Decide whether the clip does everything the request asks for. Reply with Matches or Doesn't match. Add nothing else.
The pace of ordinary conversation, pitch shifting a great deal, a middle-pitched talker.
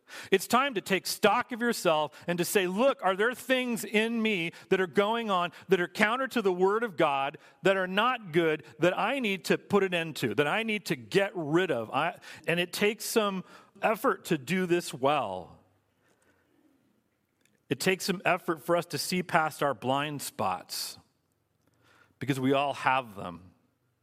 Matches